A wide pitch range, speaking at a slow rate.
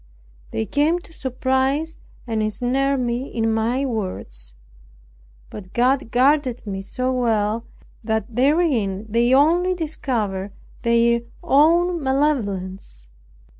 No: average, 4.5 semitones; slow, 105 wpm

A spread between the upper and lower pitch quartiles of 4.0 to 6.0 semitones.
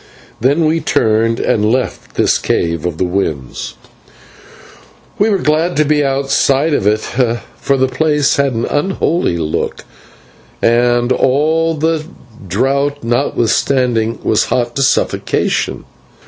Yes: average, 4.6 semitones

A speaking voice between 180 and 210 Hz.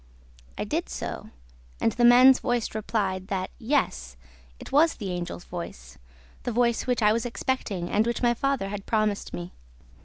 No: high, 220 Hz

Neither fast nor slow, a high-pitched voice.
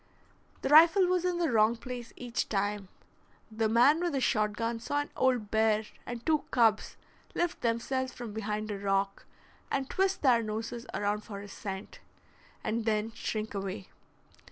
Yes: average, 165 wpm; high, 230 Hz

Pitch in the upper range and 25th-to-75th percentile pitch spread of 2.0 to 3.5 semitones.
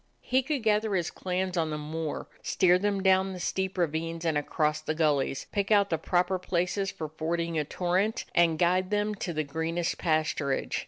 No: medium, 175 Hz; average, 3.2 semitones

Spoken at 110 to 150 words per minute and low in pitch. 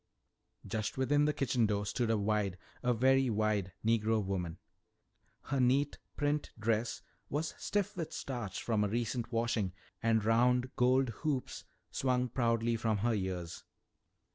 Yes: average, 140 wpm; low, 115 Hz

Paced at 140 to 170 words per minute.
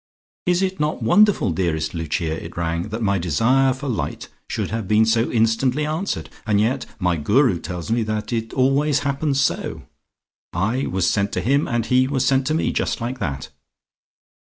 No: average, 185 wpm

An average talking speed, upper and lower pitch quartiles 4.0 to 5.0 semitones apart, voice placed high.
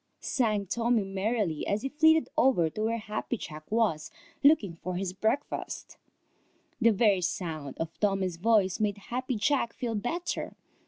Yes: average, 150 wpm; average, 4.3 semitones; high, 210 Hz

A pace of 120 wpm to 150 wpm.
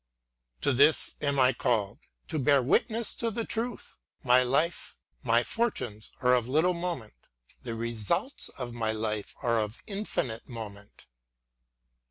Yes: average, 145 wpm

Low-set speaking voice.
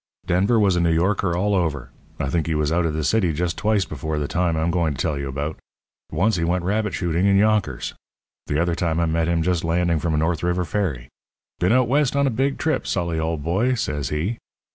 Yes: very low, 85 Hz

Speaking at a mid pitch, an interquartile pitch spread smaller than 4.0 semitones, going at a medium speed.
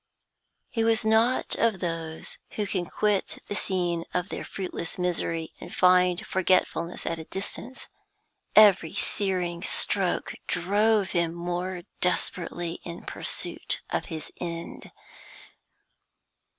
No: medium, 180 Hz; average, 2.8 semitones; slow, 115 wpm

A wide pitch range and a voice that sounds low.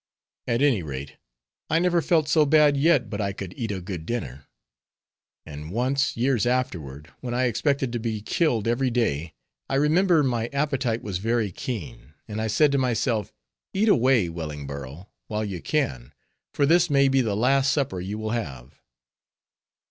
Yes: wide, 6.7 semitones; low, 115 Hz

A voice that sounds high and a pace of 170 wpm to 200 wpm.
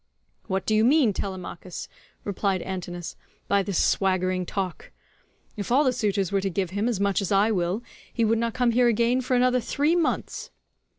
Yes: high, 200 Hz; average, 185 wpm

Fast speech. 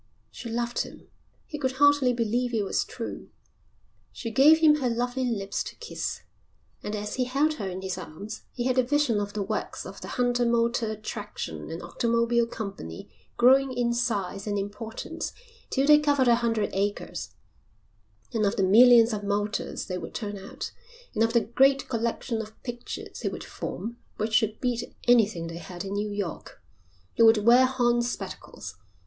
No: average, 180 wpm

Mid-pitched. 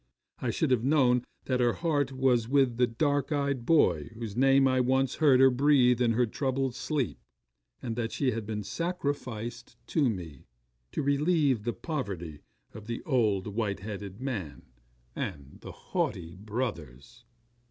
No: low, 125 Hz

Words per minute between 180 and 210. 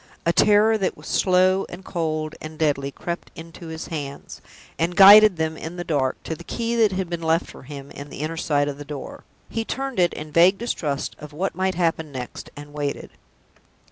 Yes: fast, 205 wpm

